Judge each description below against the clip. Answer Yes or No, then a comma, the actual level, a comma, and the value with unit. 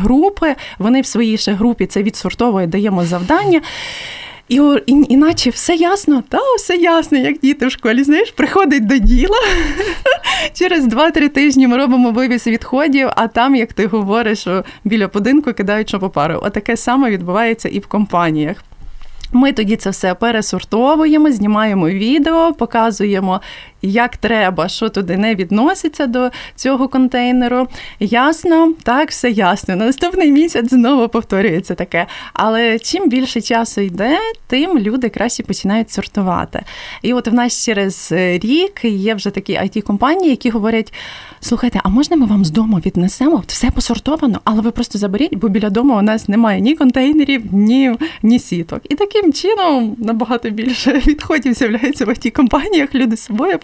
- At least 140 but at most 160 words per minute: Yes, average, 150 wpm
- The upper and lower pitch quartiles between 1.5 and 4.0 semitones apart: No, average, 5.3 semitones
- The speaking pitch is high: Yes, high, 240 Hz